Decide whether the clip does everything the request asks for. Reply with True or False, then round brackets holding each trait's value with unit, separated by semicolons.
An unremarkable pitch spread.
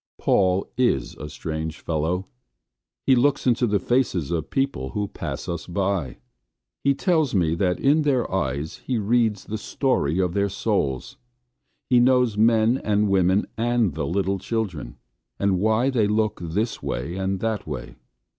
False (5.7 semitones)